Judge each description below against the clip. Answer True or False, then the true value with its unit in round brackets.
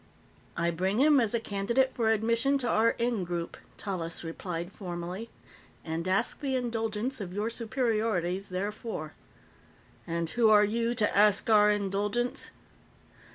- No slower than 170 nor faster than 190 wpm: False (135 wpm)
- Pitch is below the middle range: False (210 Hz)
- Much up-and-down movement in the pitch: False (4.1 semitones)